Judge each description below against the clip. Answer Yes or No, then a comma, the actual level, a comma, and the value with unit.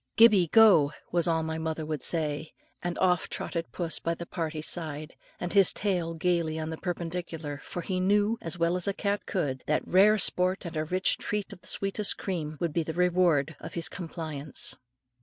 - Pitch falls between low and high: Yes, medium, 170 Hz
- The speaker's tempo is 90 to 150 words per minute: No, average, 195 wpm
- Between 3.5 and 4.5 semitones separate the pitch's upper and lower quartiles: No, narrow, 2.6 semitones